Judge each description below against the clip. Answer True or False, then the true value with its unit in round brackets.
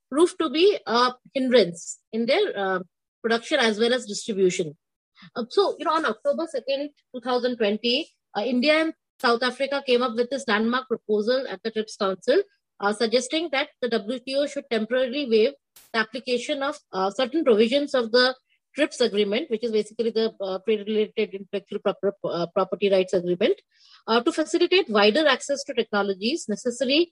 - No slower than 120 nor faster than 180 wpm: True (160 wpm)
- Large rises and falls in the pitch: False (4.9 semitones)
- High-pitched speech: True (245 Hz)